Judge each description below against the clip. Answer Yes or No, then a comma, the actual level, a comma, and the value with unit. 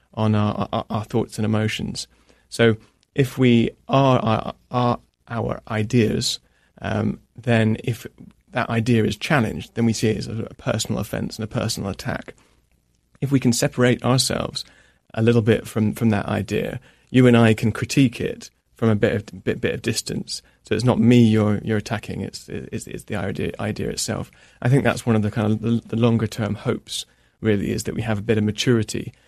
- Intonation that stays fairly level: Yes, narrow, 2.0 semitones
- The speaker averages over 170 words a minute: Yes, average, 200 wpm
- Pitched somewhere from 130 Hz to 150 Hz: No, low, 115 Hz